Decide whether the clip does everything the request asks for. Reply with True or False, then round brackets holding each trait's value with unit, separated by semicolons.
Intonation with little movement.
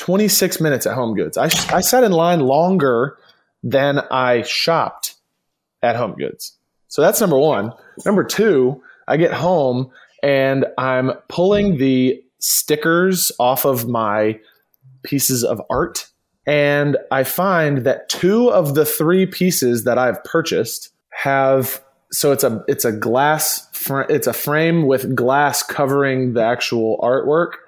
False (4.3 semitones)